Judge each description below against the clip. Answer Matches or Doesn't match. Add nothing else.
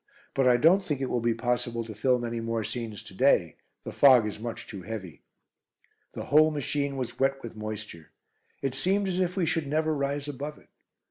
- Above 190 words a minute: Matches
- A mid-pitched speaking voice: Doesn't match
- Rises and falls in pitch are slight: Doesn't match